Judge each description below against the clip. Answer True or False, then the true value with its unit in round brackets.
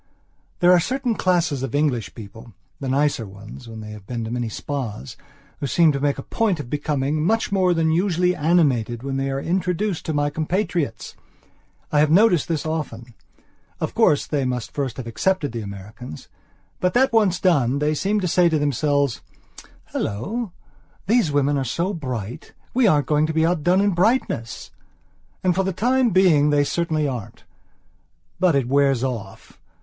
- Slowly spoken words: False (175 wpm)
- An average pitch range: False (5.9 semitones)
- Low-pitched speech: False (150 Hz)